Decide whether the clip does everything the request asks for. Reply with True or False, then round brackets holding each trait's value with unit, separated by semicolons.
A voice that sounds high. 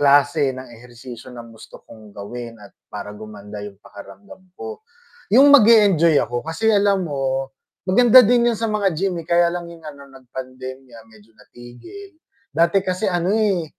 False (150 Hz)